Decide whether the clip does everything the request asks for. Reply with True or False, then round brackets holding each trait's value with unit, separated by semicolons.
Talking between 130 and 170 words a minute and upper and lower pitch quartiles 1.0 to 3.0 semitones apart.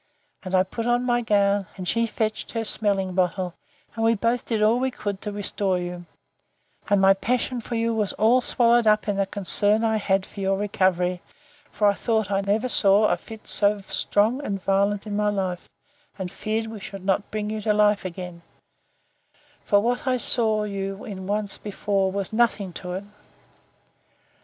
False (185 wpm; 2.5 semitones)